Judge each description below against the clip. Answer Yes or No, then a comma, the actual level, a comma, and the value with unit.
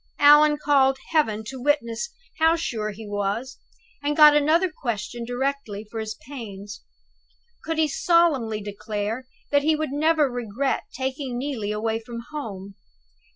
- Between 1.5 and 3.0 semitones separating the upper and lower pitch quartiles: No, average, 5.3 semitones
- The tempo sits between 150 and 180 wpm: No, average, 140 wpm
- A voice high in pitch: Yes, very high, 260 Hz